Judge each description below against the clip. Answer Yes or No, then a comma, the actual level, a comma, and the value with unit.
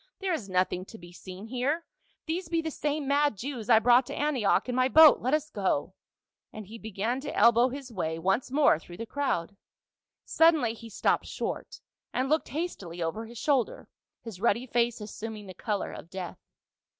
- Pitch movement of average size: No, wide, 6.1 semitones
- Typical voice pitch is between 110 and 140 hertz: No, high, 235 Hz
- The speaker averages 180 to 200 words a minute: Yes, average, 190 wpm